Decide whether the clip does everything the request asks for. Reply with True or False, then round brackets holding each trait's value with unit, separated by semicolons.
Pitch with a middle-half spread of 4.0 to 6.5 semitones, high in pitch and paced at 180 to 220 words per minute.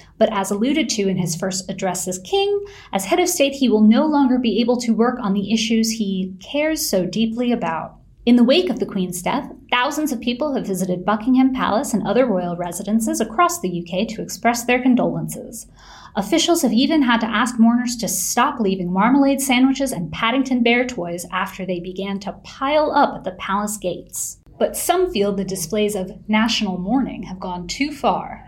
True (5.2 semitones; 225 Hz; 195 wpm)